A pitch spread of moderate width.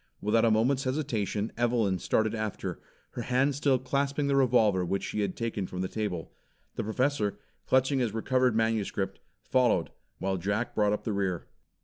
Yes: average, 4.1 semitones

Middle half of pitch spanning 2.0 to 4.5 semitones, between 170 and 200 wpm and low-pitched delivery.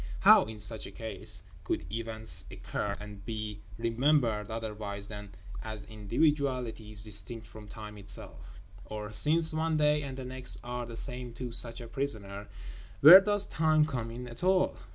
No: average, 4.1 semitones; average, 160 wpm; low, 115 Hz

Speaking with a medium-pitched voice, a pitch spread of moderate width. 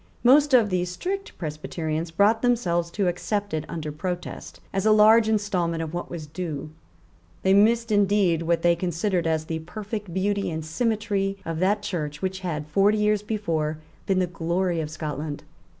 Yes: medium, 180 Hz; average, 4.2 semitones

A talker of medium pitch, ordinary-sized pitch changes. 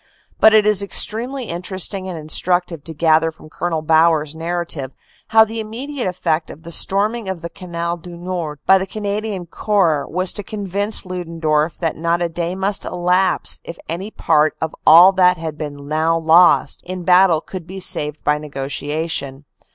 Yes: medium, 175 Hz; average, 3.2 semitones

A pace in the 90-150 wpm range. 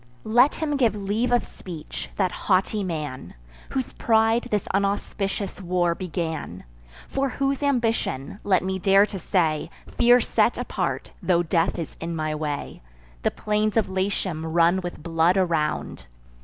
Yes: average, 145 wpm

